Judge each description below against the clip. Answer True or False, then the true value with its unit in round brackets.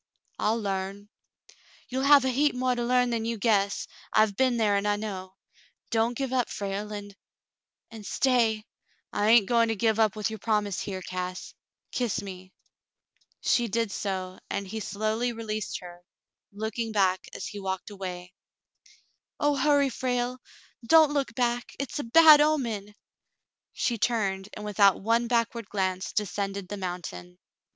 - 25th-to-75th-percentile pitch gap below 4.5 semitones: True (3.4 semitones)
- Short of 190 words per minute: True (160 wpm)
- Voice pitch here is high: True (215 Hz)